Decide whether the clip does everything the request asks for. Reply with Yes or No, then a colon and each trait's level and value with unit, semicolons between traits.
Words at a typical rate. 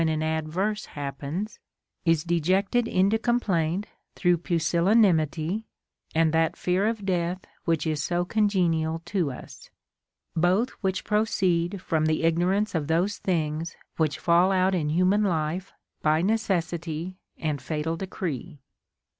No: slow, 130 wpm